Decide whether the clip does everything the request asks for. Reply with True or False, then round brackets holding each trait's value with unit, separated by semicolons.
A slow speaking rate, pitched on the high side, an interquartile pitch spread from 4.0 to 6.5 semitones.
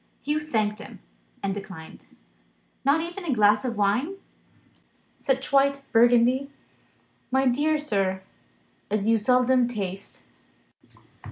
True (110 wpm; 245 Hz; 5.0 semitones)